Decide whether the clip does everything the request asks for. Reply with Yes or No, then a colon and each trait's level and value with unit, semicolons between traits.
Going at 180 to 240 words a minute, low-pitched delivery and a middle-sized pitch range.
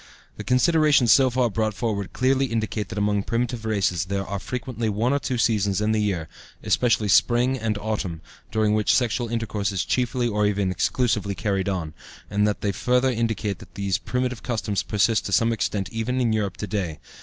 Yes: average, 190 wpm; low, 110 Hz; average, 3.2 semitones